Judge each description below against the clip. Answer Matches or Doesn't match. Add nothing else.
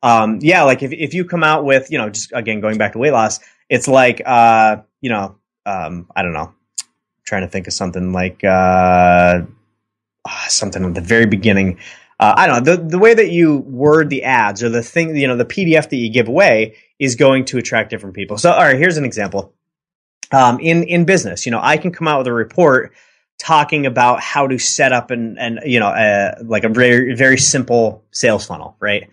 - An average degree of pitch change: Matches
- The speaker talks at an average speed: Doesn't match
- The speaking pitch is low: Matches